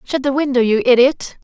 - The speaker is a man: No, female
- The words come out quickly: Yes, fast, 210 wpm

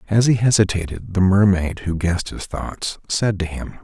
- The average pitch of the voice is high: No, very low, 95 Hz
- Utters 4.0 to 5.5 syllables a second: Yes, 4.8 syllables/s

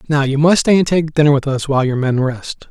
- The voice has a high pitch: No, medium, 145 Hz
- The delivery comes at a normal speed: No, fast, 290 wpm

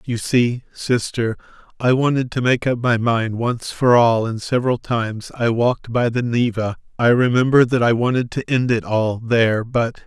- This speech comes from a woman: No, male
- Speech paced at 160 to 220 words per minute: Yes, average, 190 wpm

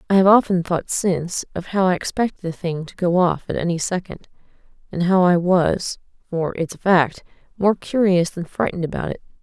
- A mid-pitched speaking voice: Yes, medium, 180 Hz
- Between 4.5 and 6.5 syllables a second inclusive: Yes, 5.4 syllables/s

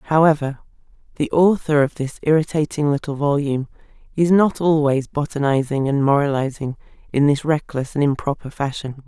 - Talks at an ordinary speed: No, slow, 130 wpm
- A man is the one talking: No, female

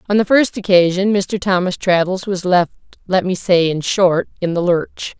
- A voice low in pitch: No, medium, 185 Hz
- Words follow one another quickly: No, average, 185 wpm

